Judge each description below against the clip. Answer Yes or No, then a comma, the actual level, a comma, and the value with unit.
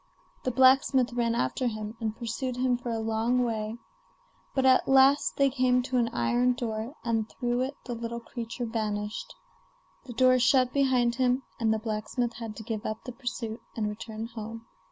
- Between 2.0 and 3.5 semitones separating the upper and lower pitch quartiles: Yes, narrow, 2.4 semitones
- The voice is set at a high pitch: Yes, high, 235 Hz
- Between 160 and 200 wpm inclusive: Yes, average, 180 wpm